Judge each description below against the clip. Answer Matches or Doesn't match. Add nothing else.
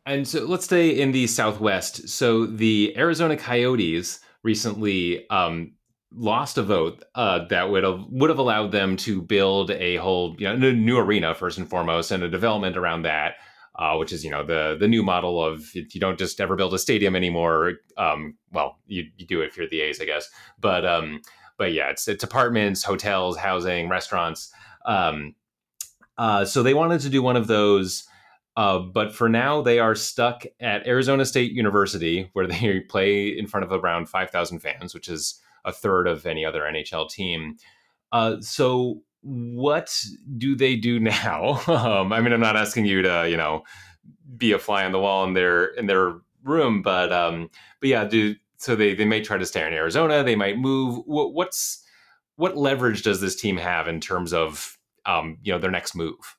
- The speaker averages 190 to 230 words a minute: Matches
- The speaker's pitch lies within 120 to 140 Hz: Doesn't match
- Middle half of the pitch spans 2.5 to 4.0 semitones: Doesn't match